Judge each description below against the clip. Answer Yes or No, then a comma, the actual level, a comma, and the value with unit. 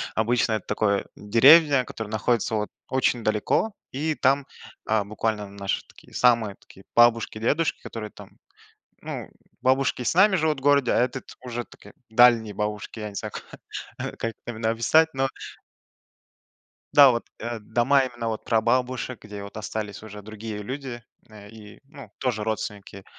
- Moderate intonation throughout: Yes, average, 3.4 semitones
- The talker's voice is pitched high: No, low, 115 Hz